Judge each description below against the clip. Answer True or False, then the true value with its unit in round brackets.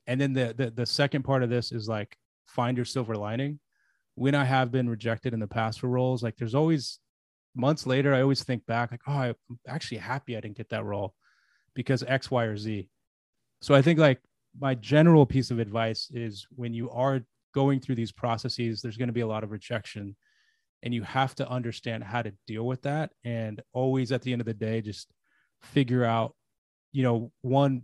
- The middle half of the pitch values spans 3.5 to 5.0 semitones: False (2.7 semitones)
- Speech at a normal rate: False (210 wpm)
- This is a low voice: True (125 Hz)